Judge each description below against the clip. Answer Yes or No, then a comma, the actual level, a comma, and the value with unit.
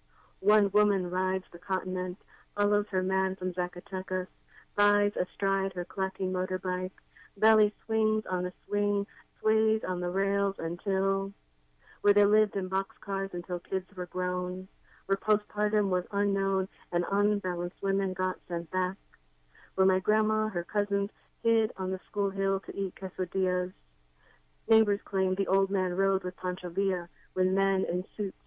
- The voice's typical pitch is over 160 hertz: Yes, high, 190 Hz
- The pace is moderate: Yes, average, 150 wpm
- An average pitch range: No, narrow, 1.7 semitones